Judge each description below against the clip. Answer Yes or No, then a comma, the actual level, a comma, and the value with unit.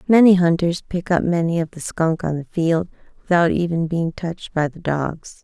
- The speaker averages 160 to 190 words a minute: No, average, 200 wpm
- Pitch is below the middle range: No, medium, 170 Hz